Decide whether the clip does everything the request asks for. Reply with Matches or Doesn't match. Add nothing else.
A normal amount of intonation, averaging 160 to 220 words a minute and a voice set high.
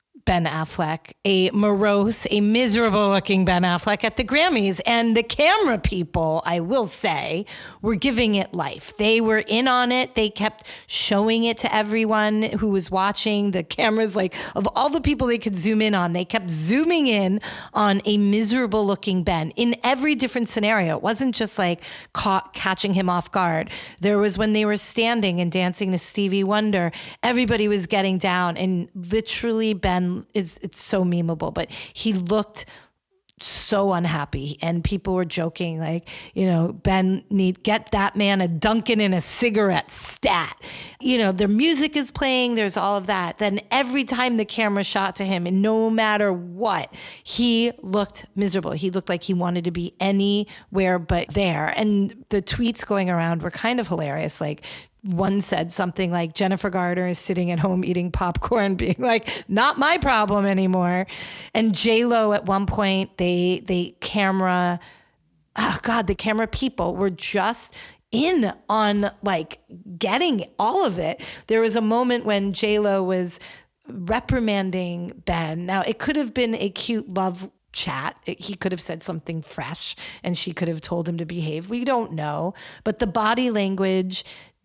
Matches